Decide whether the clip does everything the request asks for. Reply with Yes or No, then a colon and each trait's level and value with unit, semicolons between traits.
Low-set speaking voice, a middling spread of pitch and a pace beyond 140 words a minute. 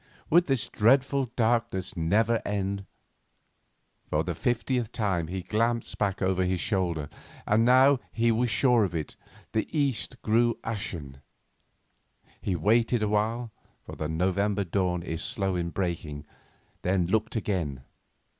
No: low, 100 Hz; average, 4.6 semitones; slow, 135 wpm